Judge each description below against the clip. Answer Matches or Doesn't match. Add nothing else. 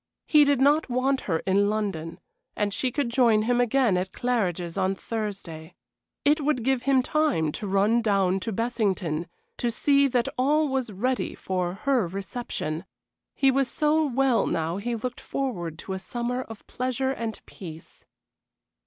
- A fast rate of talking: Doesn't match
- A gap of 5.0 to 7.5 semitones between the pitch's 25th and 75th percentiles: Matches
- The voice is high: Matches